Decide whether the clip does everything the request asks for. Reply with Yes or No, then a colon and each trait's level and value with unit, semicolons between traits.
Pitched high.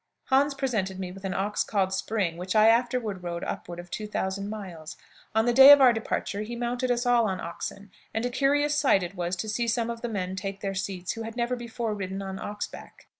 Yes: high, 210 Hz